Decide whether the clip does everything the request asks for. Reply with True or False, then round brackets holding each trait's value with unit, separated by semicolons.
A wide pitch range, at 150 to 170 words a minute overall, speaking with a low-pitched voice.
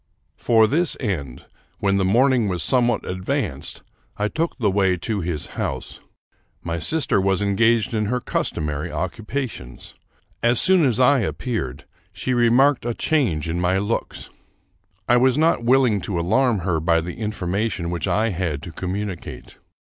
True (5.7 semitones; 165 wpm; 105 Hz)